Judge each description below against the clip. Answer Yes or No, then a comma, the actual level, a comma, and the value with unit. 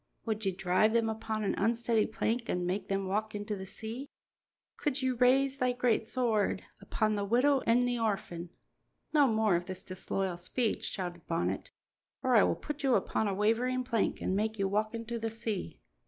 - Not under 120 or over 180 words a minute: No, average, 190 wpm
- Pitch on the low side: No, high, 220 Hz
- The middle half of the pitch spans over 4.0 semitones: No, average, 3.6 semitones